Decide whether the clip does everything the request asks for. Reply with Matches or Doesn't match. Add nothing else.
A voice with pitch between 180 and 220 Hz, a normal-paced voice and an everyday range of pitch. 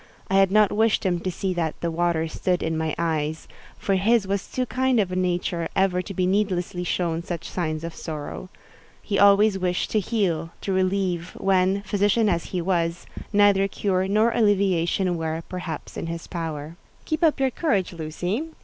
Matches